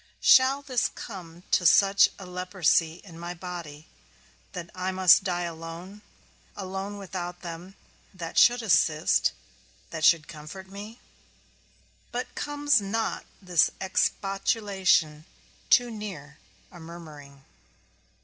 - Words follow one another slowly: Yes, slow, 110 wpm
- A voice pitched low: No, medium, 185 Hz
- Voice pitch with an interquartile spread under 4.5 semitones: Yes, average, 3.3 semitones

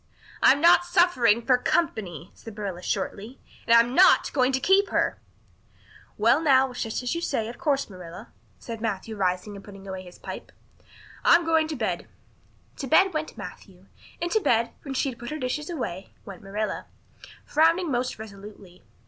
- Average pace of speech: Yes, average, 175 wpm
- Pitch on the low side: No, high, 235 Hz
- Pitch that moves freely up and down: Yes, wide, 7.3 semitones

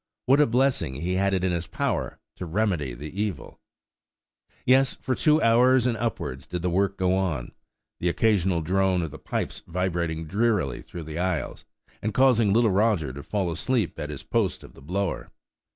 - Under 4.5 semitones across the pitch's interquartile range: No, average, 5.1 semitones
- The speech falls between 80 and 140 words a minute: No, average, 185 wpm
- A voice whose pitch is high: No, very low, 95 Hz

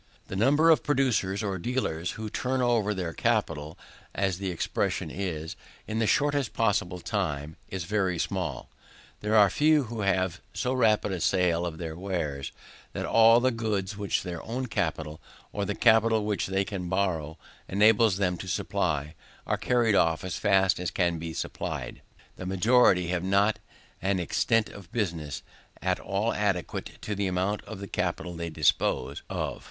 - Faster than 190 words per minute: No, average, 170 wpm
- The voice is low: Yes, very low, 95 Hz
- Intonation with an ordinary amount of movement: Yes, average, 3.9 semitones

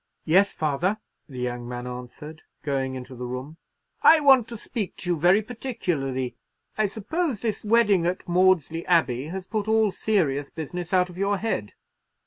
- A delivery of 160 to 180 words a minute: Yes, average, 165 wpm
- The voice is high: No, medium, 175 Hz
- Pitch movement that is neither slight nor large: No, wide, 7.6 semitones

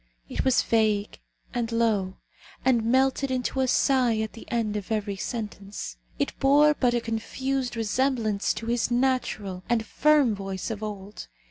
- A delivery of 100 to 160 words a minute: Yes, average, 155 wpm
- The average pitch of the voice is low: No, high, 230 Hz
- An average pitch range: Yes, average, 3.7 semitones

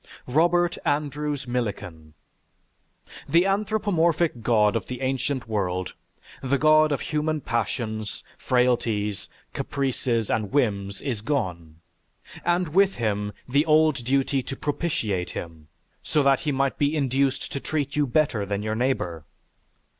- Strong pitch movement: Yes, wide, 5.9 semitones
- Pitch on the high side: No, low, 130 Hz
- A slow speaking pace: Yes, slow, 130 wpm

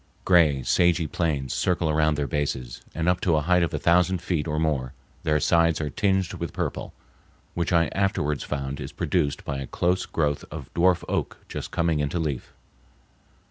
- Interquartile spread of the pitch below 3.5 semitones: Yes, average, 3.1 semitones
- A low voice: Yes, very low, 80 Hz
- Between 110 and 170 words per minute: No, average, 180 wpm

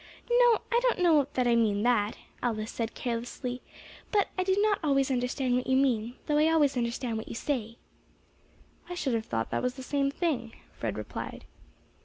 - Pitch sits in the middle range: No, very high, 255 Hz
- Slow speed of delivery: No, average, 190 wpm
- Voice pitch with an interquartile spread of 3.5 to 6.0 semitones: Yes, average, 4.4 semitones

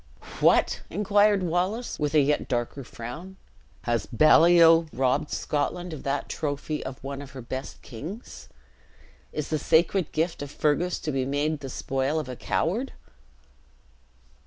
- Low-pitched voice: No, medium, 150 Hz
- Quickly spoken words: No, average, 145 wpm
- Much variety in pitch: No, average, 4.2 semitones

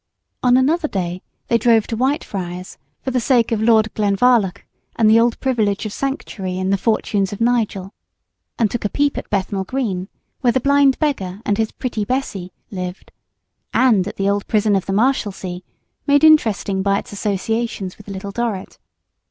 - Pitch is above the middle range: Yes, high, 215 Hz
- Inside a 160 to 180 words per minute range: Yes, average, 175 wpm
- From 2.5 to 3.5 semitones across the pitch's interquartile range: No, average, 4.0 semitones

